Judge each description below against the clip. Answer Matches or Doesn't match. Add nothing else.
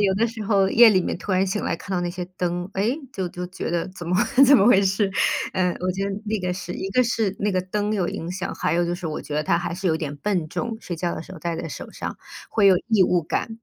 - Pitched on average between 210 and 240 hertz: Doesn't match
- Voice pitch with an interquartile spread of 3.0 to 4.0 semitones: Doesn't match